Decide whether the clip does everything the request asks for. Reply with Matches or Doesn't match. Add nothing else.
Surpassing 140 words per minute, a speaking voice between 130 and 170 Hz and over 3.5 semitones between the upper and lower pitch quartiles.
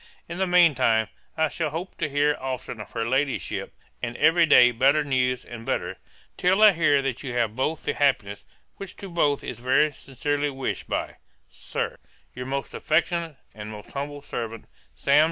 Matches